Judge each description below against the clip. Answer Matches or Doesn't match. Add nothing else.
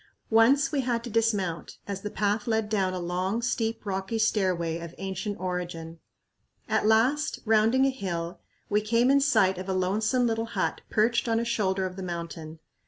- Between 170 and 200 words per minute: Matches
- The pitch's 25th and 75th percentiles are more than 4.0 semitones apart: Doesn't match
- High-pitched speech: Matches